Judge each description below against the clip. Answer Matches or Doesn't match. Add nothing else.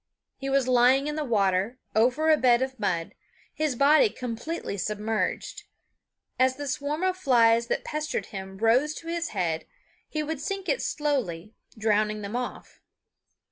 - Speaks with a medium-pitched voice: Doesn't match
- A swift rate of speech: Doesn't match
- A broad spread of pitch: Matches